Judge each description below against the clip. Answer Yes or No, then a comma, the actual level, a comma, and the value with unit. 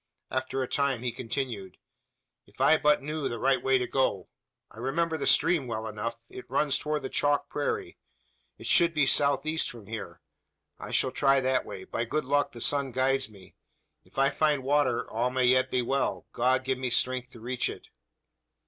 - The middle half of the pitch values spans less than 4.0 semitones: Yes, narrow, 2.5 semitones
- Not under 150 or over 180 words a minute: No, average, 195 wpm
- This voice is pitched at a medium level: No, low, 130 Hz